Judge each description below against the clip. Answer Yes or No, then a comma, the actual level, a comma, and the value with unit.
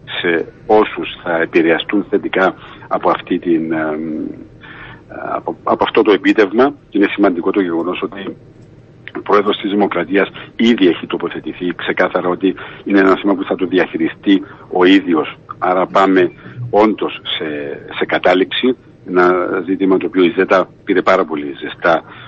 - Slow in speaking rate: No, average, 145 wpm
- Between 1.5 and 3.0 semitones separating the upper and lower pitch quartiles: Yes, narrow, 2.5 semitones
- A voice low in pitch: Yes, very low, 95 Hz